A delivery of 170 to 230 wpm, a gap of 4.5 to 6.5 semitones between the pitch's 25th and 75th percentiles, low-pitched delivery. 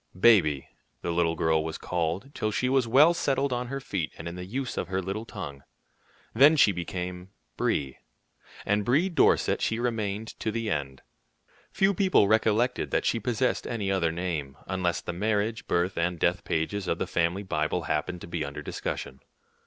Yes: average, 180 wpm; wide, 5.6 semitones; very low, 95 Hz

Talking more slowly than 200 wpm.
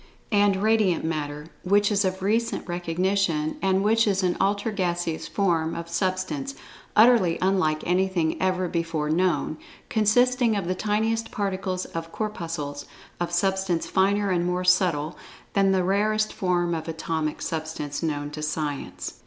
Yes: average, 145 wpm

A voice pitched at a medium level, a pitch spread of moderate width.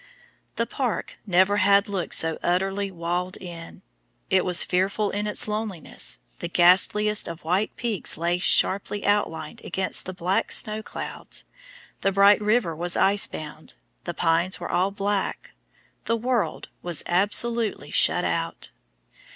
No: high, 195 Hz; average, 3.0 semitones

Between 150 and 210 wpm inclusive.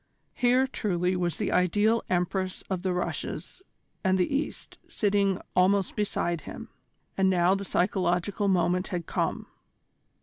No: slow, 135 wpm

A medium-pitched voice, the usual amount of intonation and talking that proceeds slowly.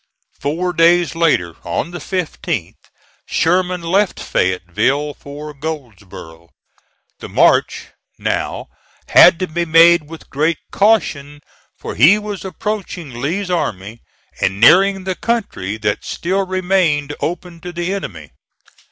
Yes: medium, 165 Hz; average, 4.8 semitones; slow, 120 wpm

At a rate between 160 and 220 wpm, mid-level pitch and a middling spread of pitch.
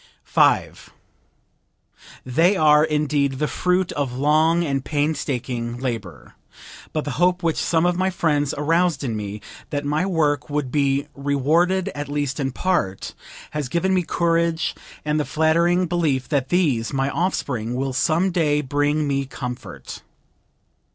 No: average, 140 wpm; medium, 150 Hz; average, 3.6 semitones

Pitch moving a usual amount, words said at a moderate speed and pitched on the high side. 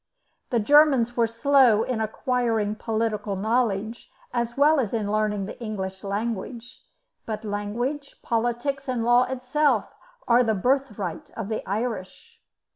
No: average, 3.1 semitones; slow, 130 wpm; high, 230 Hz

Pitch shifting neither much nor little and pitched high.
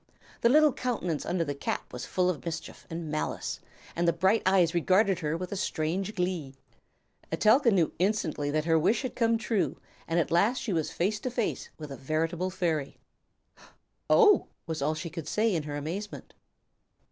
No: average, 5.0 semitones; medium, 175 Hz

